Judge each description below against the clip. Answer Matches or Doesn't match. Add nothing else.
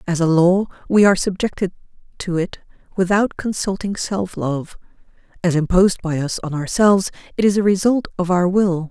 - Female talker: Matches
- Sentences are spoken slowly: Doesn't match